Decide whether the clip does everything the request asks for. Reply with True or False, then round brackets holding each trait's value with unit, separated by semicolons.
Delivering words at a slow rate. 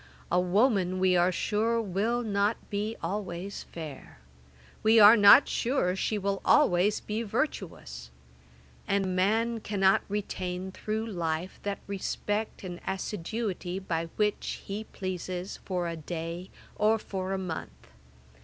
True (130 wpm)